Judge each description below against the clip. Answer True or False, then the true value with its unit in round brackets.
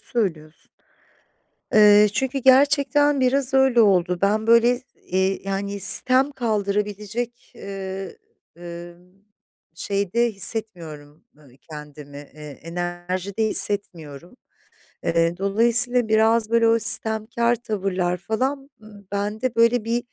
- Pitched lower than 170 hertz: False (210 Hz)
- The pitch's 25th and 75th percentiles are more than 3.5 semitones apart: True (4.6 semitones)